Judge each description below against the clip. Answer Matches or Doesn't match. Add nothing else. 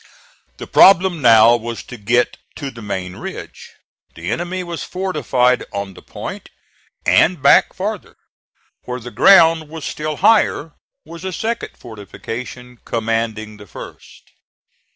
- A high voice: Doesn't match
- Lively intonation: Matches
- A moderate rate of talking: Doesn't match